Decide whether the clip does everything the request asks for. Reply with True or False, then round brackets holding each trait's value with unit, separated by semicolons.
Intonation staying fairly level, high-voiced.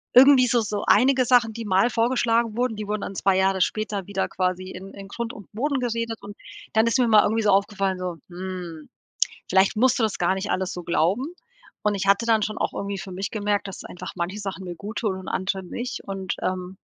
False (3.2 semitones; 205 Hz)